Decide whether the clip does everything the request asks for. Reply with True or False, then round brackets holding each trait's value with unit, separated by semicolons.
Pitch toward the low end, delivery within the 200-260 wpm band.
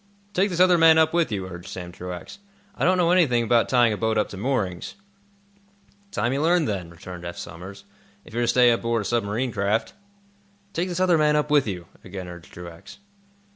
True (115 Hz; 205 wpm)